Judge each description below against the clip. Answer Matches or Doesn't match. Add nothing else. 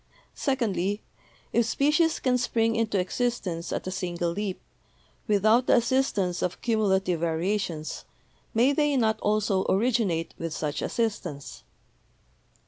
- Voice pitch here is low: Doesn't match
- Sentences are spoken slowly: Matches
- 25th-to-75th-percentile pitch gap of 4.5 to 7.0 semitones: Matches